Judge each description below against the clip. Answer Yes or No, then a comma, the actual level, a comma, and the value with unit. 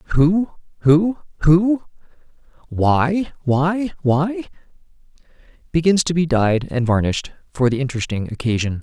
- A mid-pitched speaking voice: Yes, medium, 150 Hz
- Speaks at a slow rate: Yes, slow, 110 wpm